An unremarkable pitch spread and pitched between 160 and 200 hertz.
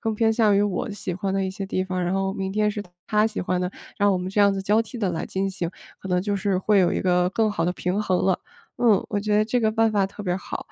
No: narrow, 2.2 semitones; high, 195 Hz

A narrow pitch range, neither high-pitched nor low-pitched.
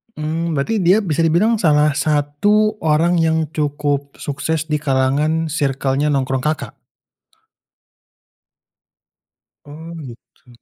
Yes: narrow, 2.3 semitones; medium, 150 Hz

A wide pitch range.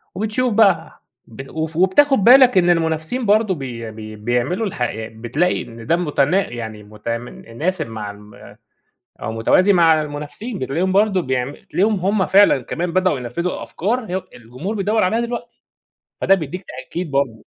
Yes: wide, 8.3 semitones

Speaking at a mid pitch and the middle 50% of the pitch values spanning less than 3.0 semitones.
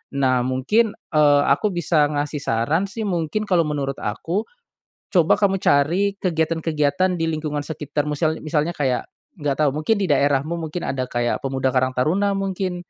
No: medium, 155 Hz; average, 4.0 semitones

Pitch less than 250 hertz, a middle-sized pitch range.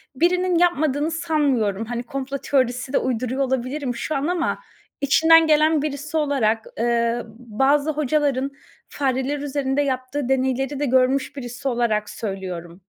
No: very high, 270 Hz; average, 3.3 semitones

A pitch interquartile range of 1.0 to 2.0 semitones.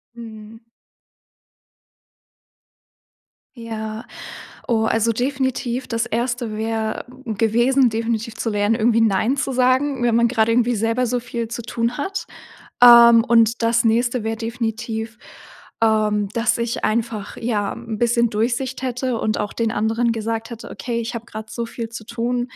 Yes: narrow, 1.5 semitones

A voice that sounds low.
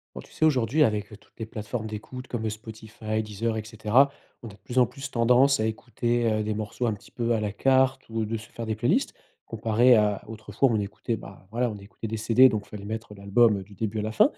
Yes: low, 110 Hz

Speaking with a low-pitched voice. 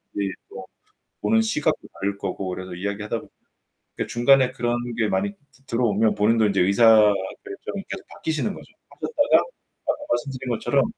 Yes: low, 110 Hz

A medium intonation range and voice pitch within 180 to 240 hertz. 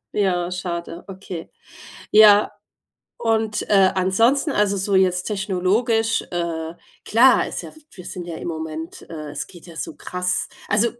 Yes: average, 3.5 semitones; high, 190 Hz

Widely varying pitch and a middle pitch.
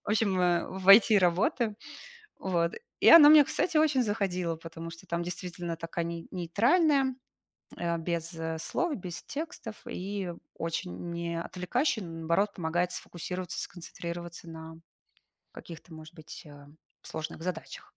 No: average, 3.7 semitones; medium, 175 Hz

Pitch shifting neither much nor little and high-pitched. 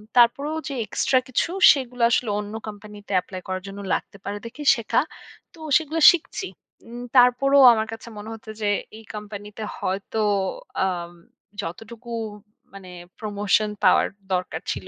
Yes: average, 3.3 semitones; high, 220 Hz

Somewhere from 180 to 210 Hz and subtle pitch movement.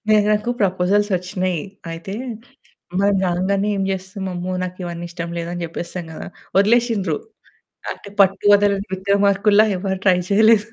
Yes: high, 195 Hz; narrow, 2.2 semitones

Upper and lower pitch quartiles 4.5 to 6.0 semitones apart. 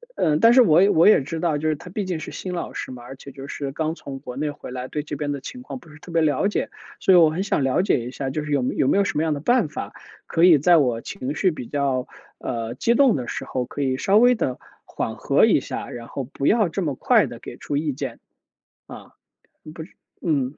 Yes: average, 4.9 semitones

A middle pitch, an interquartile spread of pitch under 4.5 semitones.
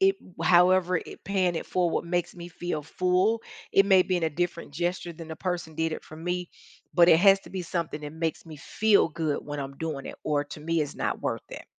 Yes: medium, 170 Hz; narrow, 2.4 semitones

